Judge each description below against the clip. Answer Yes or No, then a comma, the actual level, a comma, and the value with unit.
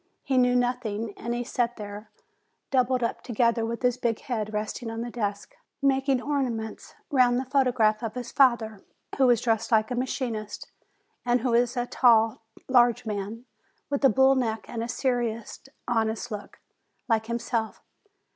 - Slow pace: No, average, 170 wpm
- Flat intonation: Yes, narrow, 2.1 semitones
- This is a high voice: Yes, high, 235 Hz